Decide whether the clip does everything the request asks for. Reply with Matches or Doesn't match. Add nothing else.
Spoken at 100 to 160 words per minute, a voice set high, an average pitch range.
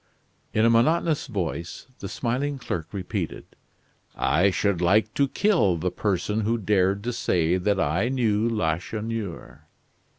Doesn't match